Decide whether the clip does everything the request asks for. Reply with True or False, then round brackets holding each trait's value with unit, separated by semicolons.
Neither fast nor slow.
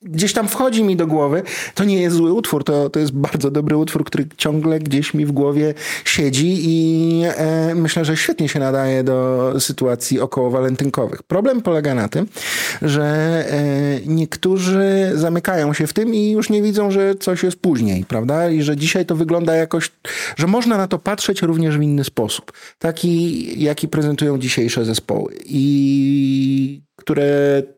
False (165 wpm)